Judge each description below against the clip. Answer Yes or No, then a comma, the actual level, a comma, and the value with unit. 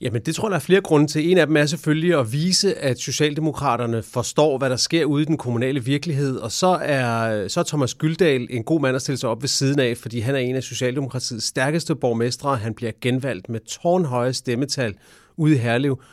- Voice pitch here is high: No, low, 135 Hz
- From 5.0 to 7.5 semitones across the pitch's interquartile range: No, average, 4.1 semitones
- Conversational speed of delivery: No, fast, 225 wpm